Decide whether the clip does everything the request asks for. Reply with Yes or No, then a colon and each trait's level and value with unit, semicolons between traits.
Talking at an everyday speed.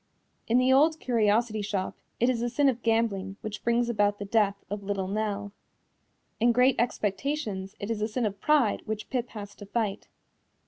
Yes: average, 185 wpm